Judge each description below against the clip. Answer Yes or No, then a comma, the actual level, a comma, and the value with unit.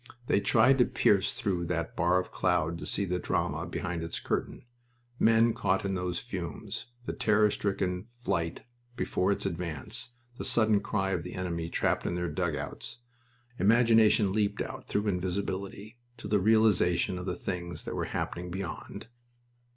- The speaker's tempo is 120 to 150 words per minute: No, average, 160 wpm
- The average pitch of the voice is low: Yes, very low, 95 Hz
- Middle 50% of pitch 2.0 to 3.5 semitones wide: Yes, average, 3.1 semitones